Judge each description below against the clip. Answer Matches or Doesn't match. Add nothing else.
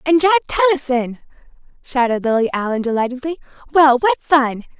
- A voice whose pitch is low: Doesn't match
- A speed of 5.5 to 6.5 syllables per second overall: Matches